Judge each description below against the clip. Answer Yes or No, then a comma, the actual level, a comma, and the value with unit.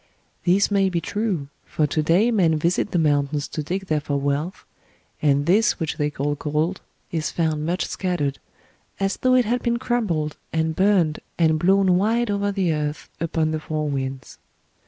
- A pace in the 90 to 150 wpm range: No, average, 180 wpm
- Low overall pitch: No, medium, 165 Hz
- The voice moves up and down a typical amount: Yes, average, 4.4 semitones